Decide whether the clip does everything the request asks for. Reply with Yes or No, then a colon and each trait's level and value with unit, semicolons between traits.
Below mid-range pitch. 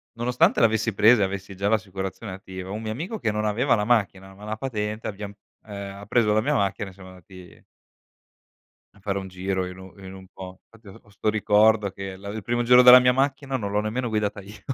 Yes: low, 105 Hz